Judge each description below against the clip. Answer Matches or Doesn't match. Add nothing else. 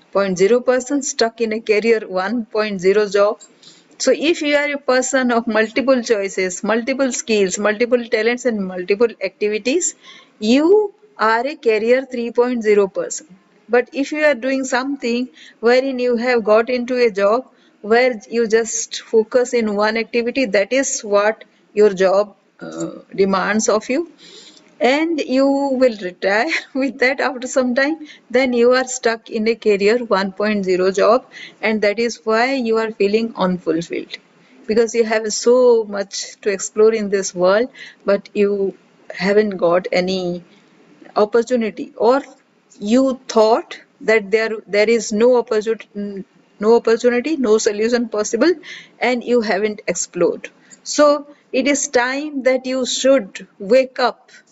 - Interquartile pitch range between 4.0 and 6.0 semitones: Doesn't match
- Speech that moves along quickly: Doesn't match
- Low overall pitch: Doesn't match